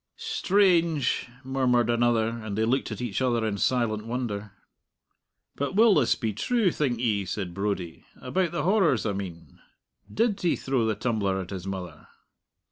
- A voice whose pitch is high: No, low, 120 Hz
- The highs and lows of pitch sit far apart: Yes, wide, 6.5 semitones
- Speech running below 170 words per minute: Yes, average, 160 wpm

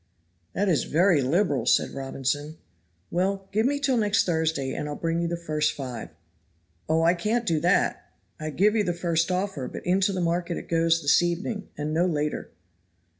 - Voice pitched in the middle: Yes, medium, 170 Hz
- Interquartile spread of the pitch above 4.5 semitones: No, average, 4.1 semitones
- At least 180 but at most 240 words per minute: Yes, average, 185 wpm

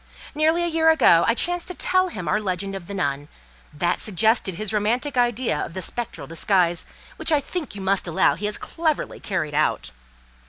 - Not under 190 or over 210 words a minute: Yes, average, 200 wpm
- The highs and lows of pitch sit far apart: Yes, wide, 8.8 semitones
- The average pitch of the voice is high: Yes, high, 210 Hz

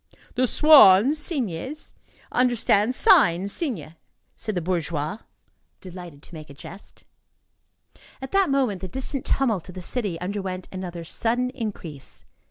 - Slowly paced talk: Yes, slow, 130 wpm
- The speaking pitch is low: No, high, 200 Hz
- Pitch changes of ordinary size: No, wide, 6.5 semitones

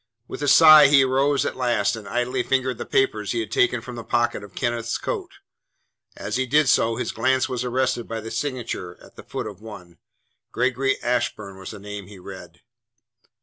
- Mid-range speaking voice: No, low, 120 Hz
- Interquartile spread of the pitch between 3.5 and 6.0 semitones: Yes, average, 3.8 semitones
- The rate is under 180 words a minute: No, average, 195 wpm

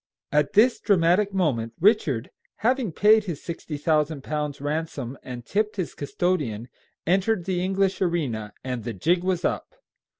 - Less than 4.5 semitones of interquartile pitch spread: No, wide, 5.5 semitones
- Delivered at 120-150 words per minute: Yes, average, 145 wpm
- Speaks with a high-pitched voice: No, medium, 165 Hz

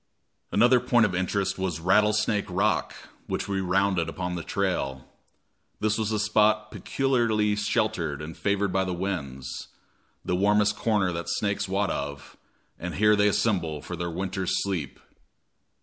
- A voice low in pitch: Yes, low, 100 Hz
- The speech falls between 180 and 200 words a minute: No, average, 150 wpm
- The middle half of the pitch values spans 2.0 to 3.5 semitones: Yes, average, 3.1 semitones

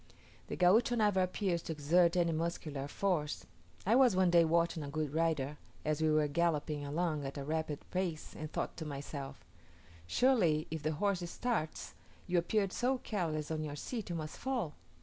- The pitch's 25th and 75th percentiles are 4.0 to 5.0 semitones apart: No, average, 3.3 semitones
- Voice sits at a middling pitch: Yes, medium, 165 Hz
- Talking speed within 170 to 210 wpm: Yes, average, 180 wpm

